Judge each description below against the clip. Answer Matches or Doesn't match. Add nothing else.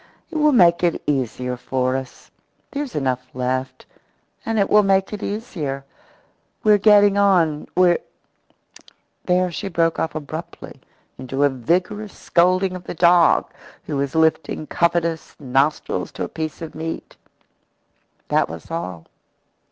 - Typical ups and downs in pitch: Doesn't match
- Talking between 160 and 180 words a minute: Doesn't match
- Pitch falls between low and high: Matches